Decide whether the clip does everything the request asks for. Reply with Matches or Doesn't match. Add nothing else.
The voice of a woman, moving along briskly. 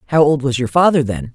Matches